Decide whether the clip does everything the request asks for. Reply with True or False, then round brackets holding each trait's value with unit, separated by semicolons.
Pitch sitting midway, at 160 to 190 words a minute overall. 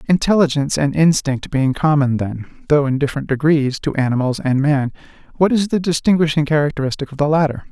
True (145 Hz; 170 wpm)